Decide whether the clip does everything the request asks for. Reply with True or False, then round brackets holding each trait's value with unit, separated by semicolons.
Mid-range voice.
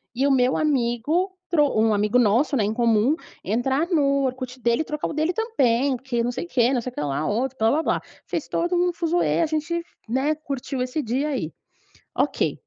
False (265 Hz)